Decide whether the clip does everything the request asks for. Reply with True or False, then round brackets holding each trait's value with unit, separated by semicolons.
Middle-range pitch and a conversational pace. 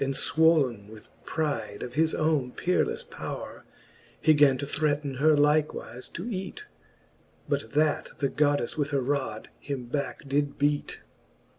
True (145 Hz; 150 wpm)